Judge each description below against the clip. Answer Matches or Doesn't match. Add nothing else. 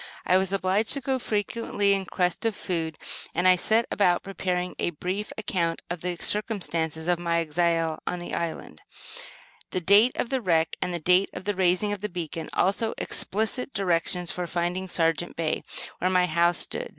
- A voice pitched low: Doesn't match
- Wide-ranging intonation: Doesn't match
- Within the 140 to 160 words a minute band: Doesn't match